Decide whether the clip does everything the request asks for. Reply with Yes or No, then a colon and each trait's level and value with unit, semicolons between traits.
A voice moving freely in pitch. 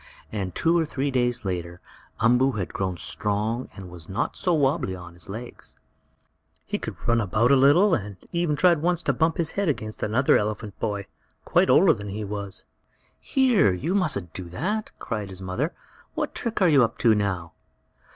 Yes: wide, 7.4 semitones